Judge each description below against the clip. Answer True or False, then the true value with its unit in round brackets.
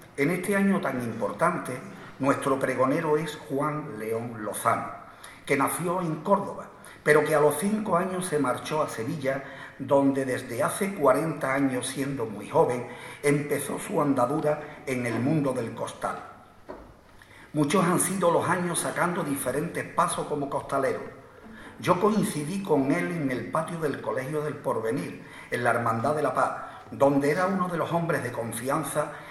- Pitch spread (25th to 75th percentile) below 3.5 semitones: False (4.0 semitones)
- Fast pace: False (155 wpm)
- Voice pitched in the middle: True (150 Hz)